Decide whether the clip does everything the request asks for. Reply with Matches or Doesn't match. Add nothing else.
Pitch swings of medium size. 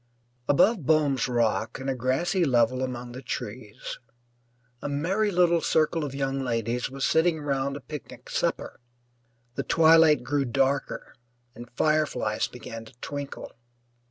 Matches